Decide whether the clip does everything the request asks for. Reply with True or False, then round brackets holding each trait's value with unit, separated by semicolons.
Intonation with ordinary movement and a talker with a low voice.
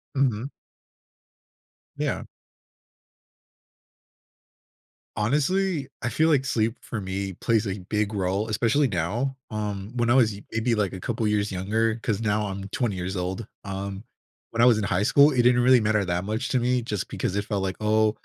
True (3.5 semitones; 110 Hz)